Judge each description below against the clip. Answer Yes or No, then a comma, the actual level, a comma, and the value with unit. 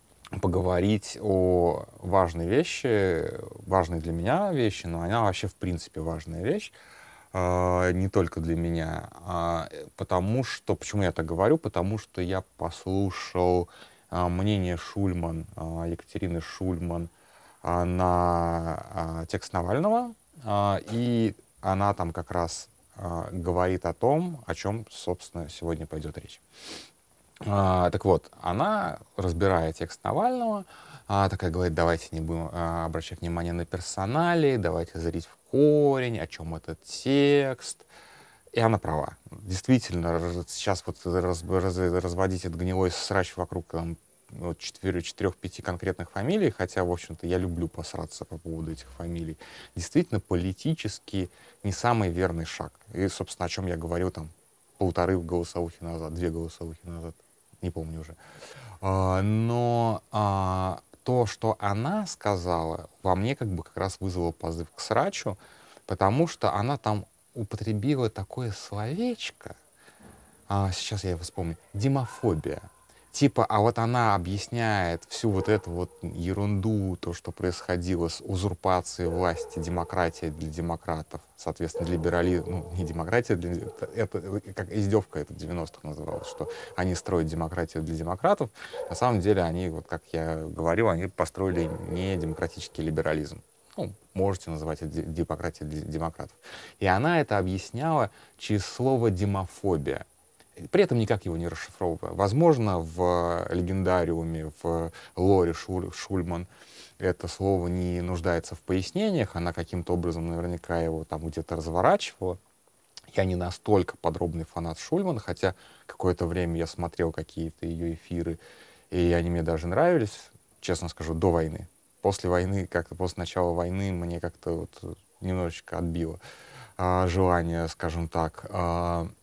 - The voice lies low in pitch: Yes, very low, 90 Hz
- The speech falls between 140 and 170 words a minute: No, average, 130 wpm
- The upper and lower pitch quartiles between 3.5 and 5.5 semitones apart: No, average, 3.0 semitones